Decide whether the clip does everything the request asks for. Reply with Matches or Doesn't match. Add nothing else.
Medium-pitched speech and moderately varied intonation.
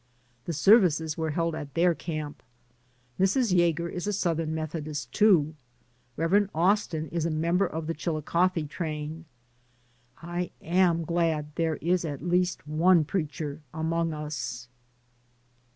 Doesn't match